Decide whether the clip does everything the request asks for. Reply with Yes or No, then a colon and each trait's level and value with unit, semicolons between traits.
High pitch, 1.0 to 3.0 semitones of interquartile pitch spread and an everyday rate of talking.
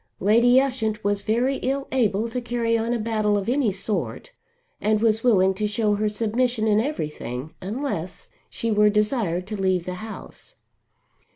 Yes: high, 215 Hz; average, 2.7 semitones; average, 165 wpm